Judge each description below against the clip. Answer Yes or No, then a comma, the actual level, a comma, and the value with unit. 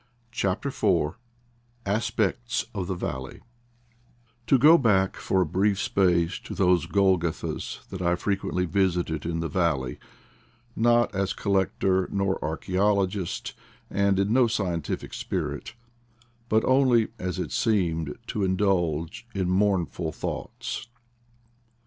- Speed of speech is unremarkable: No, slow, 120 wpm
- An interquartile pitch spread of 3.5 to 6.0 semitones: No, average, 3.1 semitones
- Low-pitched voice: Yes, very low, 95 Hz